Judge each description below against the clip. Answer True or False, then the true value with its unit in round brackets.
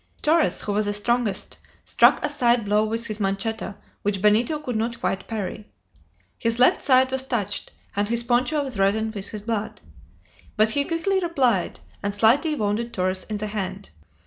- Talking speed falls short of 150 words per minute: False (175 wpm)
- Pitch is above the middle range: True (220 Hz)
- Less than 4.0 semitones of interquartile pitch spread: True (3.4 semitones)